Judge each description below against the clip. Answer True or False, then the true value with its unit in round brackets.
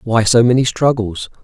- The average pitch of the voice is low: True (120 Hz)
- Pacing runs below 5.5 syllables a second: True (4.7 syllables/s)